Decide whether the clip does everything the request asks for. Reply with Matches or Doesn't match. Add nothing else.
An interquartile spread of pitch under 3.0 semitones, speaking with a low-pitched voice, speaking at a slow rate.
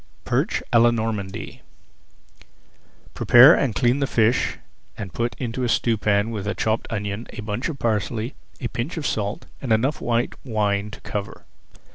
Doesn't match